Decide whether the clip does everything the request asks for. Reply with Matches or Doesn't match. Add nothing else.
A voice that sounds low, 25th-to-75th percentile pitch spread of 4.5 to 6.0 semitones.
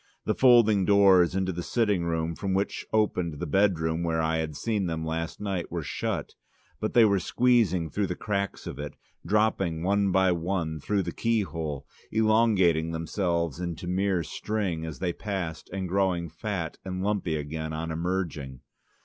Doesn't match